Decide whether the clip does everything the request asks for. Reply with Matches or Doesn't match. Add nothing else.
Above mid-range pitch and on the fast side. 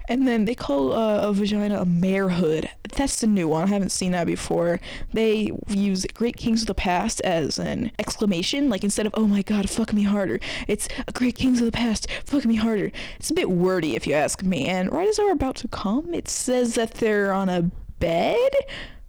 Matches